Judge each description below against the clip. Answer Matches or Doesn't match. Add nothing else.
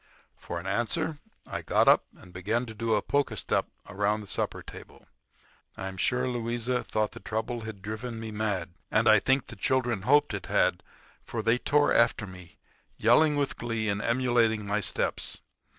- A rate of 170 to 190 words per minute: Matches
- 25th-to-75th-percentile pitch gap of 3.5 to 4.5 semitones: Doesn't match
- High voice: Doesn't match